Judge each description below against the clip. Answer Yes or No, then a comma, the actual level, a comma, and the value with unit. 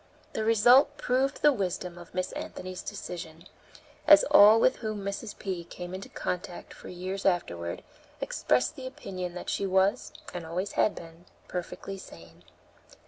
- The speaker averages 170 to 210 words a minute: No, average, 150 wpm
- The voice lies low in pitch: No, medium, 185 Hz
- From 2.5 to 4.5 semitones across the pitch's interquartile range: Yes, average, 3.3 semitones